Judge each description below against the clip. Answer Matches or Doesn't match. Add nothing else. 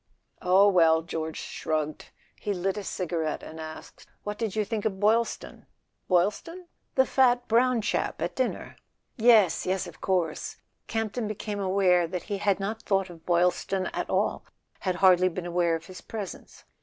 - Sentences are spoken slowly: Doesn't match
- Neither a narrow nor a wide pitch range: Matches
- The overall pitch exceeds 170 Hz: Matches